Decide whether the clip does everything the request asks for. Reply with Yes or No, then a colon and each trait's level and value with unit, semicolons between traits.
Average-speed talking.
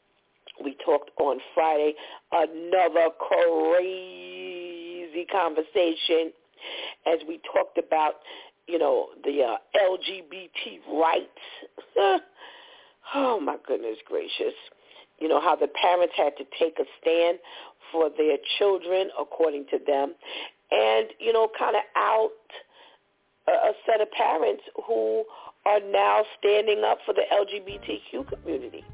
No: slow, 120 wpm